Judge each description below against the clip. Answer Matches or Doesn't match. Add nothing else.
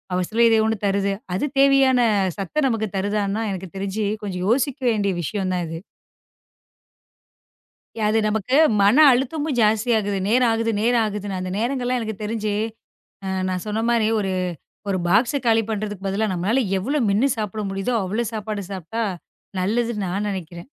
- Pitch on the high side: Matches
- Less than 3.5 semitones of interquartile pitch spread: Matches